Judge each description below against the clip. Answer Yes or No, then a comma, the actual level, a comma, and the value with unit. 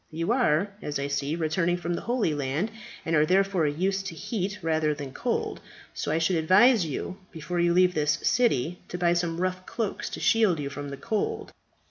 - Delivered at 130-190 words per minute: No, average, 200 wpm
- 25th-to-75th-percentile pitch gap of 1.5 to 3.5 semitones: No, average, 4.1 semitones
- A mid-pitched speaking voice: Yes, medium, 170 Hz